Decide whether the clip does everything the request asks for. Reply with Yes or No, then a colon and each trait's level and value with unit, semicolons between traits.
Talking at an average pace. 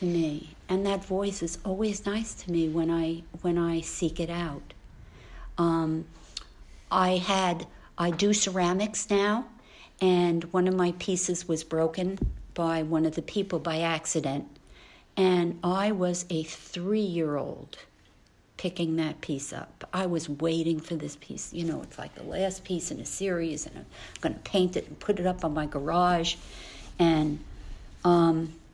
Yes: average, 165 wpm